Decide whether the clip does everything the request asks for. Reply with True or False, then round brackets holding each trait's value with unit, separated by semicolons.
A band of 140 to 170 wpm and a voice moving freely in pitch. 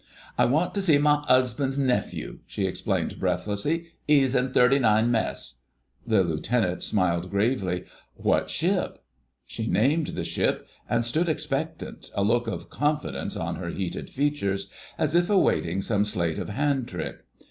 True (145 wpm; 6.6 semitones)